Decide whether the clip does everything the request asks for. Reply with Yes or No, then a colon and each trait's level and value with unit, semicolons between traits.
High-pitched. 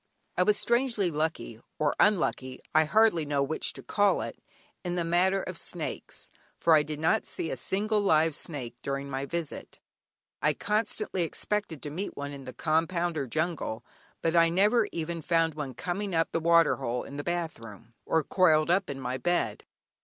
No: medium, 165 Hz